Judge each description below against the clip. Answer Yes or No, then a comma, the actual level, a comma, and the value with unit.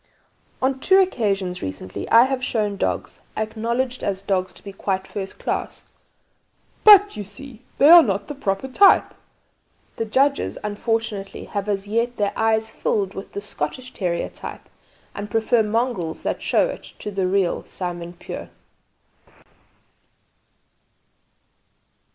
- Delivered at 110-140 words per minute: Yes, slow, 135 wpm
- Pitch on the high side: Yes, high, 210 Hz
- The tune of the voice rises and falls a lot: No, average, 4.2 semitones